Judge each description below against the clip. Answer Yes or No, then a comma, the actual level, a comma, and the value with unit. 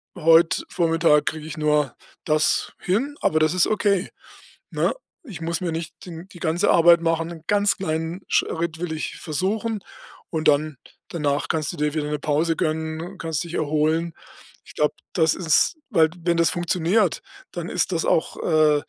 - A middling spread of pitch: No, narrow, 2.0 semitones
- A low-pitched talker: No, medium, 165 Hz